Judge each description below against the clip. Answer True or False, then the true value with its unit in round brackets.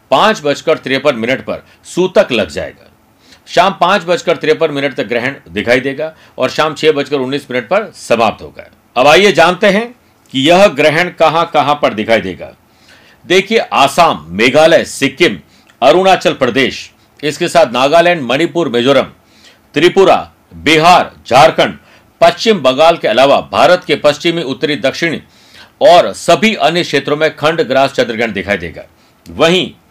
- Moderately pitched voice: True (155 Hz)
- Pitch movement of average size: True (4.0 semitones)